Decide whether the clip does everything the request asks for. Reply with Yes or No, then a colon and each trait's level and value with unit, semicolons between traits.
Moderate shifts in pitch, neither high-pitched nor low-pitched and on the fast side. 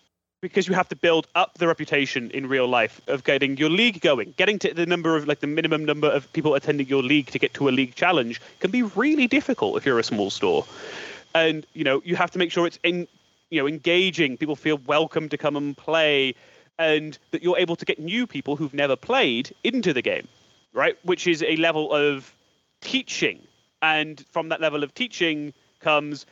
Yes: average, 3.5 semitones; medium, 160 Hz; fast, 210 wpm